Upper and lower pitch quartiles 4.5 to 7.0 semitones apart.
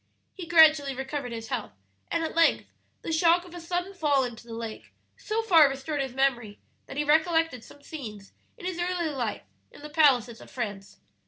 Yes: average, 5.2 semitones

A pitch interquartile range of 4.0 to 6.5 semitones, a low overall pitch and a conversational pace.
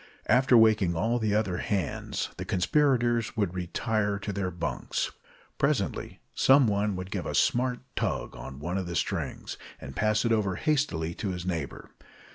Yes: average, 4.6 semitones; low, 105 Hz; average, 165 wpm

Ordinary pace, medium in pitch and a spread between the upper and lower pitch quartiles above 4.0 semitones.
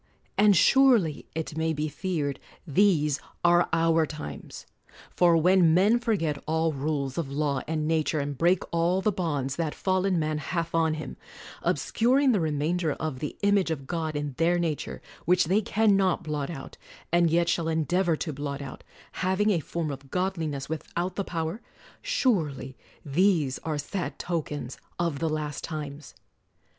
No: average, 165 wpm; medium, 160 Hz; average, 3.4 semitones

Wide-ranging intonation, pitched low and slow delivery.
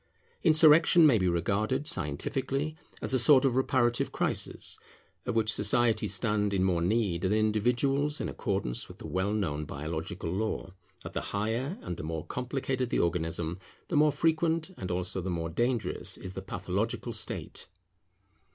No: wide, 6.5 semitones; low, 110 Hz; average, 160 wpm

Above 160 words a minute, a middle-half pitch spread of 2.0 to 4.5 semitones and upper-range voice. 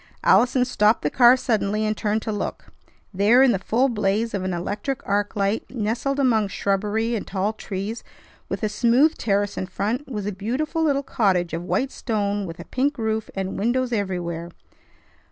Yes: average, 180 wpm; average, 3.6 semitones; high, 215 Hz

